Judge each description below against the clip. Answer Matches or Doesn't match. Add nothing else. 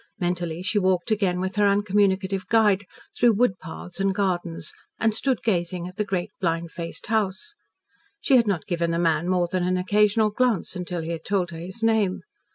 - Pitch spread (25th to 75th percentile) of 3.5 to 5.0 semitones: Doesn't match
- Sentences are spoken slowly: Doesn't match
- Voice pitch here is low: Doesn't match